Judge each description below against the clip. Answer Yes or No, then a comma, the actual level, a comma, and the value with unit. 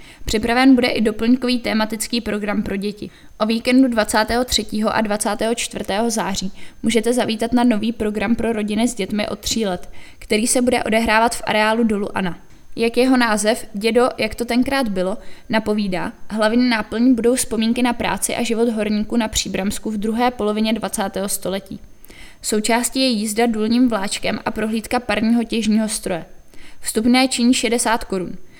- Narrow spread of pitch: Yes, narrow, 2.1 semitones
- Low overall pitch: No, high, 225 Hz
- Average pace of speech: Yes, average, 155 wpm